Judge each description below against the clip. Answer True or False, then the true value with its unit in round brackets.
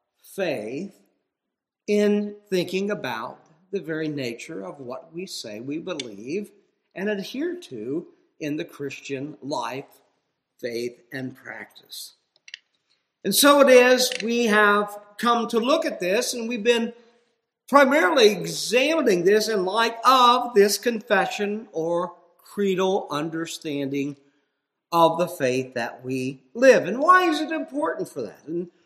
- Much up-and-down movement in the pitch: True (7.2 semitones)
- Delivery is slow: True (130 wpm)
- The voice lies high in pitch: True (200 Hz)